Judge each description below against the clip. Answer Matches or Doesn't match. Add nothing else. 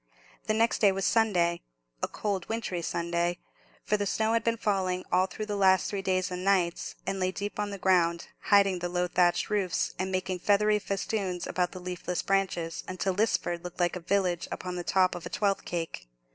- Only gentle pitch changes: Matches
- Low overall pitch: Doesn't match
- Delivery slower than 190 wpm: Doesn't match